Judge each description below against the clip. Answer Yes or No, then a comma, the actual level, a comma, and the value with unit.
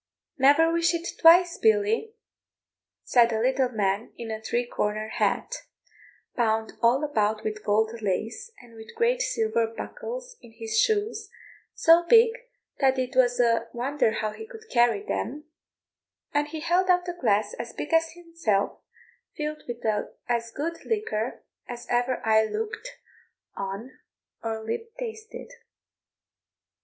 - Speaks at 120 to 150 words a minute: Yes, average, 140 wpm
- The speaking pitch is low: No, high, 245 Hz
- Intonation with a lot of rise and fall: Yes, wide, 7.4 semitones